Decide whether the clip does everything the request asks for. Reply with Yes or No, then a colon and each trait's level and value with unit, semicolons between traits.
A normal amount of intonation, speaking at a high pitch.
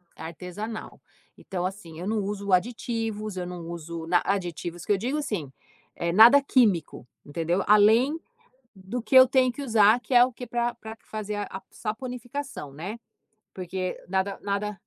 Yes: average, 4.7 semitones; high, 205 Hz